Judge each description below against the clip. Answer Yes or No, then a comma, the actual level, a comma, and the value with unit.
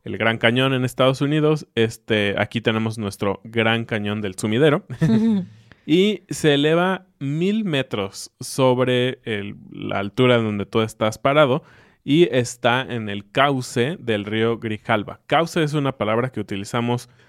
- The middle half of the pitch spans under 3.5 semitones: No, average, 4.5 semitones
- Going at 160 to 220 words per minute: No, average, 140 wpm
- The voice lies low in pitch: Yes, low, 120 Hz